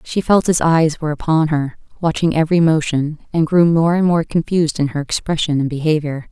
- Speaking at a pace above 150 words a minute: Yes, average, 200 wpm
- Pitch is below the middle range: No, medium, 160 Hz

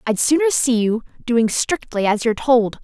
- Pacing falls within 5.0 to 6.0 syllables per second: No, 4.8 syllables/s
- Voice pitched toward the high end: Yes, high, 240 Hz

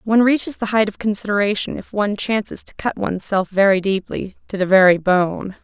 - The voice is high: Yes, high, 200 Hz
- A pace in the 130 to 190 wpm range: No, average, 200 wpm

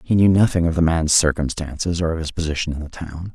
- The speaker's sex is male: Yes, male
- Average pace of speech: No, fast, 250 wpm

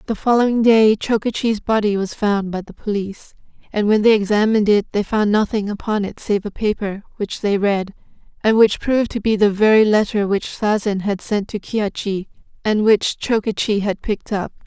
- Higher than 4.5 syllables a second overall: Yes, 5.2 syllables/s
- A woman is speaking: Yes, female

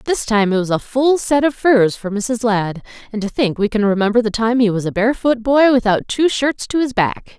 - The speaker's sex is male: No, female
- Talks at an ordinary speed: No, fast, 250 wpm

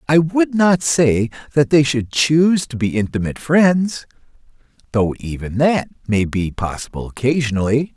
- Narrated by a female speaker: No, male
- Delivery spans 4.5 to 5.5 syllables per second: Yes, 4.6 syllables/s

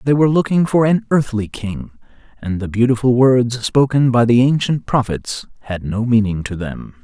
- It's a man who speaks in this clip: Yes, male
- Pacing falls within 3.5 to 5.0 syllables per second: Yes, 4.9 syllables/s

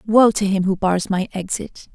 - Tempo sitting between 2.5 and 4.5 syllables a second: No, 4.7 syllables/s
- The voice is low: No, high, 195 Hz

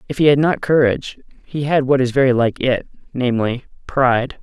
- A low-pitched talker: Yes, low, 130 Hz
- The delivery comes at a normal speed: Yes, average, 190 wpm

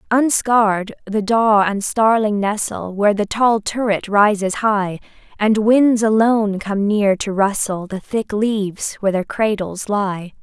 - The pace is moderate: Yes, average, 150 wpm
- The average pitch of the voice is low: No, high, 210 Hz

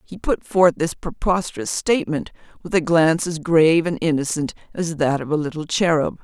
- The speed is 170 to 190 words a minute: Yes, average, 185 wpm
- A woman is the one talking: Yes, female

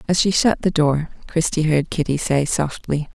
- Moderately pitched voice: Yes, medium, 155 Hz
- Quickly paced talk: No, average, 190 wpm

